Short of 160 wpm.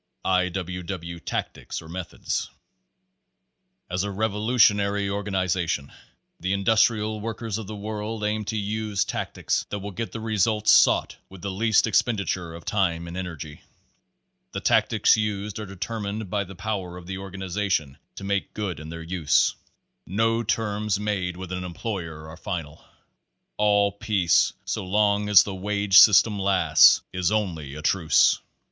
Yes: average, 150 wpm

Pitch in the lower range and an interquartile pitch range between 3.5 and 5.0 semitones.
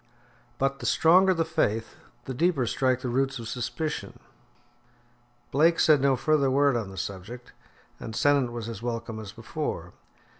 Yes: low, 130 Hz; average, 3.9 semitones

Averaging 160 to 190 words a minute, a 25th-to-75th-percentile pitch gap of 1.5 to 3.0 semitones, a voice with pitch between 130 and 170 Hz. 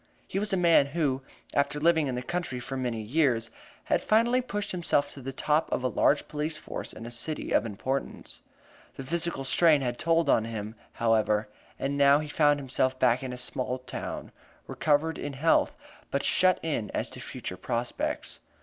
No: average, 185 wpm; average, 4.5 semitones; medium, 140 Hz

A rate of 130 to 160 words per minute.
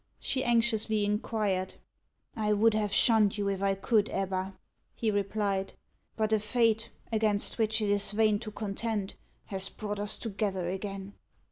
Yes: average, 150 wpm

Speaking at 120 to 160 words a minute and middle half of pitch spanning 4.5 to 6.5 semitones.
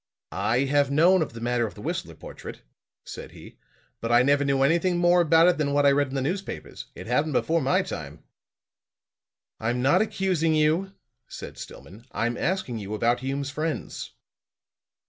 No: average, 175 wpm; average, 5.1 semitones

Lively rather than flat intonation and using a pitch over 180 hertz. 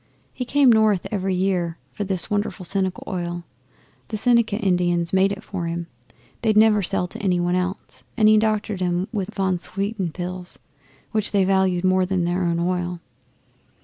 No: narrow, 2.6 semitones; high, 190 Hz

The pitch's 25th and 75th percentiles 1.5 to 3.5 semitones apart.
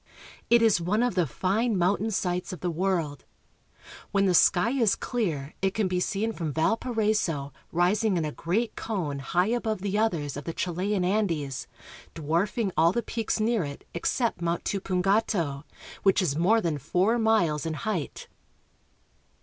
No: average, 4.7 semitones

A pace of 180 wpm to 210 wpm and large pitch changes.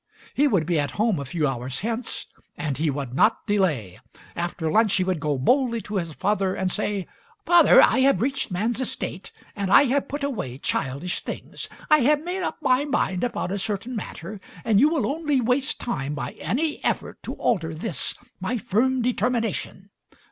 Yes: average, 185 wpm; wide, 7.4 semitones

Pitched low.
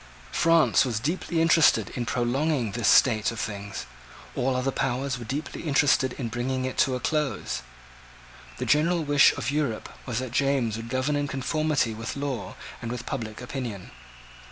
Yes: low, 130 Hz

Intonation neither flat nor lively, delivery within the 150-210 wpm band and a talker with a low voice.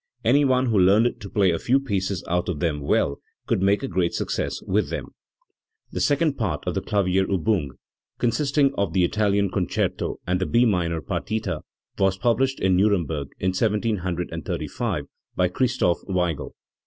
Yes: average, 4.1 semitones; average, 160 wpm; very low, 95 Hz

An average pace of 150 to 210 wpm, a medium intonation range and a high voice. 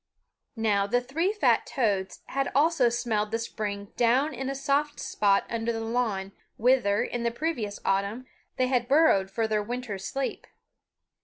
Yes: average, 160 wpm; average, 4.3 semitones; high, 235 Hz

